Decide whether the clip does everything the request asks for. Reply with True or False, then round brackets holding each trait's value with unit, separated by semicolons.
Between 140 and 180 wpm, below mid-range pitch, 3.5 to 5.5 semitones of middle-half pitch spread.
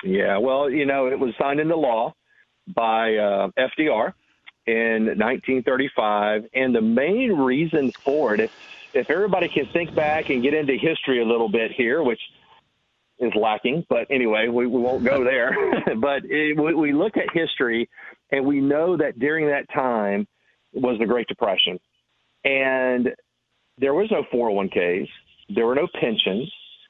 True (160 wpm; 130 Hz; 4.5 semitones)